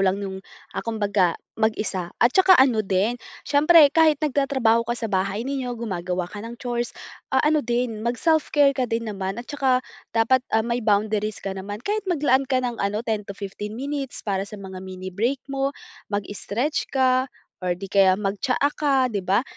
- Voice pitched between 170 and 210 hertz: No, high, 230 Hz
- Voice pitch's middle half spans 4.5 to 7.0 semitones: Yes, average, 5.1 semitones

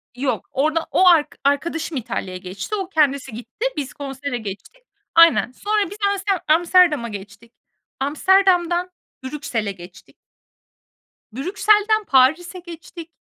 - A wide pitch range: Yes, wide, 6.2 semitones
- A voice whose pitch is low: No, very high, 305 Hz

